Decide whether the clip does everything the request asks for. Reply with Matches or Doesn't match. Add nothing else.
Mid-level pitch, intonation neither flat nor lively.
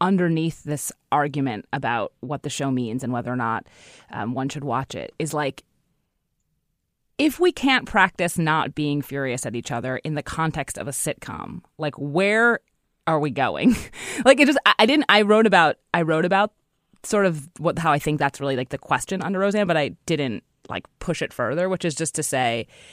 Doesn't match